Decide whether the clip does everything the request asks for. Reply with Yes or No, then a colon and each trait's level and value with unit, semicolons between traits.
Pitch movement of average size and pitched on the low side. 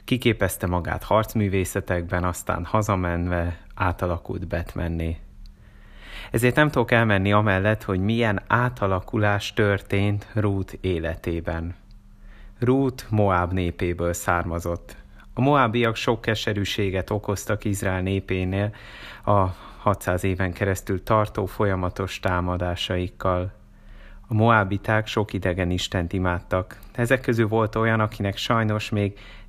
Yes: average, 3.1 semitones; low, 100 Hz